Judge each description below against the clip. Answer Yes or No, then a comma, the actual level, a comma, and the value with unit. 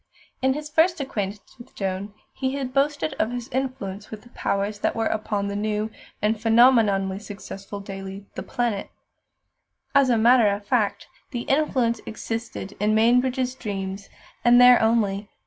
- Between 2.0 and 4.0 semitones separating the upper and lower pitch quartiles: Yes, average, 3.7 semitones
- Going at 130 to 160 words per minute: Yes, average, 155 wpm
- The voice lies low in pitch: No, high, 220 Hz